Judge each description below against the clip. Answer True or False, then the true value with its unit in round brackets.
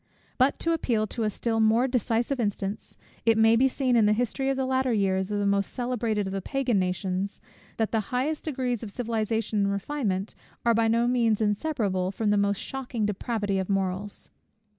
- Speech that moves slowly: False (195 wpm)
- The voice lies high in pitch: True (225 Hz)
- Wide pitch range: False (3.6 semitones)